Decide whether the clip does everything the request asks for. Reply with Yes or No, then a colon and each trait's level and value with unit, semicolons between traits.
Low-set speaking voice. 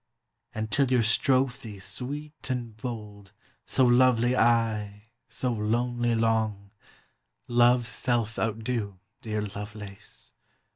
Yes: low, 115 Hz